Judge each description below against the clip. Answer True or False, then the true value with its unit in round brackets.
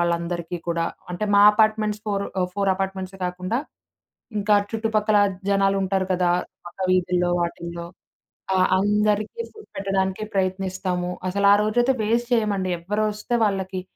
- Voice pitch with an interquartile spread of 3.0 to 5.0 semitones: False (2.5 semitones)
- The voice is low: False (195 Hz)